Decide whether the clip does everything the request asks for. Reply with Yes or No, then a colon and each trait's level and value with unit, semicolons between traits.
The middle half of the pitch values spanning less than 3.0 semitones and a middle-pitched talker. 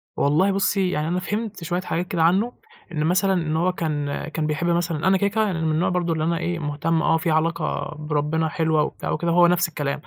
Yes: narrow, 2.5 semitones; medium, 165 Hz